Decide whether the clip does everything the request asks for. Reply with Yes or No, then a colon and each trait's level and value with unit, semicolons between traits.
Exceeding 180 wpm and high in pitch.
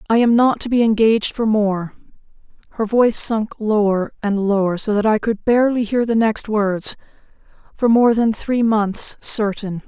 No: average, 165 wpm; high, 215 Hz